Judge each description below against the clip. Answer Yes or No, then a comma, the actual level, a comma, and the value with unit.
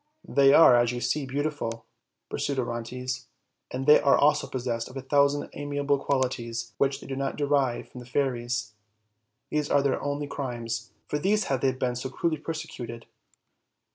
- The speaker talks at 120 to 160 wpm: No, average, 170 wpm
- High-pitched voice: No, low, 135 Hz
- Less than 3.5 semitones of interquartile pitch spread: Yes, average, 2.8 semitones